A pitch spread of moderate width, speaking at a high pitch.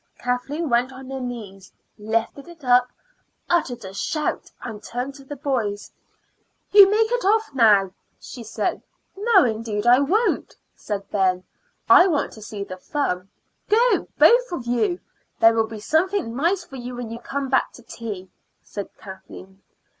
No: wide, 6.2 semitones; high, 245 Hz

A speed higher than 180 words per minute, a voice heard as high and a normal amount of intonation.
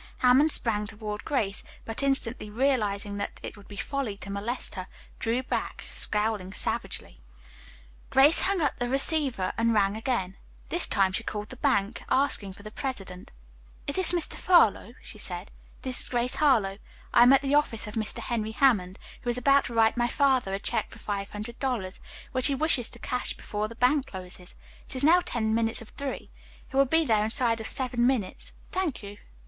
Yes: average, 195 wpm; high, 230 Hz; average, 4.4 semitones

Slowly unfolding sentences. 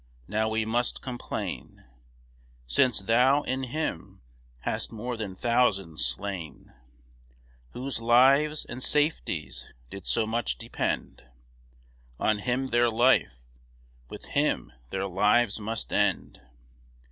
Yes: slow, 110 wpm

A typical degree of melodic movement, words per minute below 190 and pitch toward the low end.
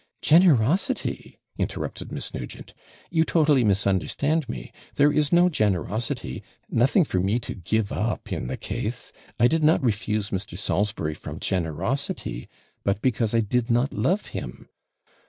No: wide, 6.8 semitones; average, 140 wpm; low, 115 Hz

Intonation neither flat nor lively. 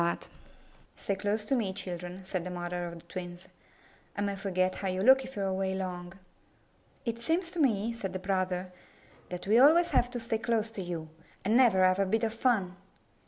Yes: average, 3.8 semitones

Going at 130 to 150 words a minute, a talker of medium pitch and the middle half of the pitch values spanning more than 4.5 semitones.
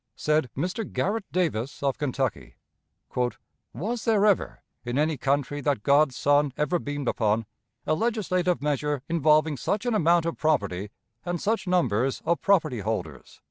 Yes: average, 145 wpm; medium, 150 Hz; average, 5.1 semitones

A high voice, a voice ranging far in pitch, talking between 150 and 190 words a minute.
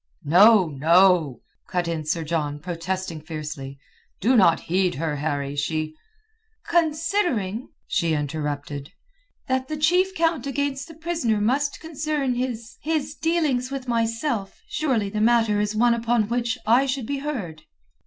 No: high, 220 Hz; wide, 8.9 semitones; average, 140 wpm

